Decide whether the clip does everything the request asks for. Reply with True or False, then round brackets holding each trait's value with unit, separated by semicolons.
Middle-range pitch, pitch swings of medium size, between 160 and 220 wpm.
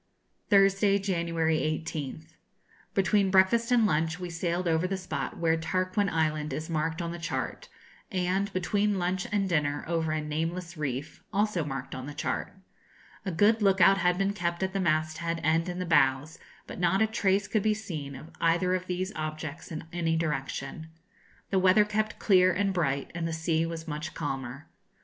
True (170 Hz; 3.4 semitones; 180 wpm)